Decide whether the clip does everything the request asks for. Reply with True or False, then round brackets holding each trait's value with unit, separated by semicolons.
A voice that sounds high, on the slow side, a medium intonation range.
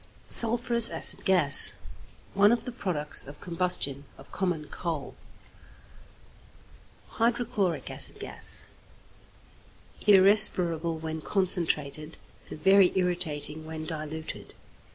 False (175 Hz; 90 wpm; 4.2 semitones)